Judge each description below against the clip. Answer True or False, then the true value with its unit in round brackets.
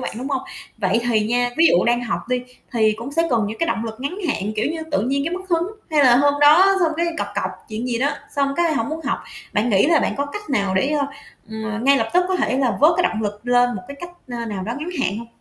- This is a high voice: True (250 Hz)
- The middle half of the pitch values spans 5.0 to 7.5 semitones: True (5.4 semitones)